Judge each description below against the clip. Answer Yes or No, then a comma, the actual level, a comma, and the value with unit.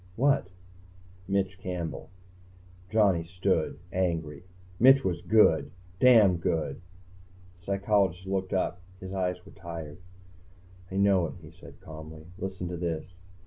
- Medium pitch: No, very low, 90 Hz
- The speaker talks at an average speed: No, slow, 130 wpm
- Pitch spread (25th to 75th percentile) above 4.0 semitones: No, average, 2.8 semitones